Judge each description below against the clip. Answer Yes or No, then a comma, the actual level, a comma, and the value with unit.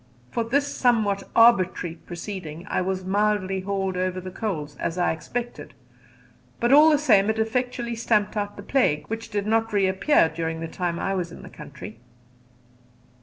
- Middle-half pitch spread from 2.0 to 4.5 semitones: Yes, average, 4.1 semitones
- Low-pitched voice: No, high, 200 Hz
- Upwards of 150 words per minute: Yes, average, 170 wpm